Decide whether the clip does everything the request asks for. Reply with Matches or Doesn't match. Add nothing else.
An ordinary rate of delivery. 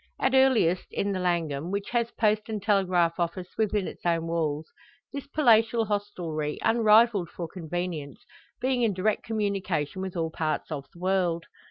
Matches